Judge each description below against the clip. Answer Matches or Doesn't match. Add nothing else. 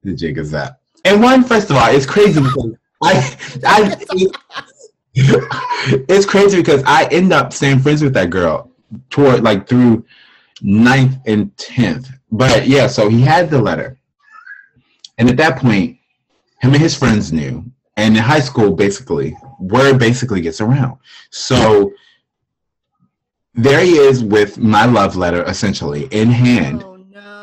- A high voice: Doesn't match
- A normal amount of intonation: Doesn't match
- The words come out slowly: Doesn't match